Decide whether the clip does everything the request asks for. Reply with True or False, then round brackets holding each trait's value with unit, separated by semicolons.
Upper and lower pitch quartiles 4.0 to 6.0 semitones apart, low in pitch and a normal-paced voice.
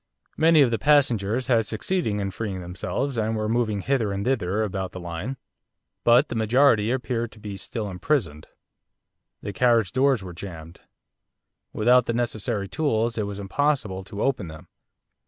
True (4.3 semitones; 110 Hz; 160 wpm)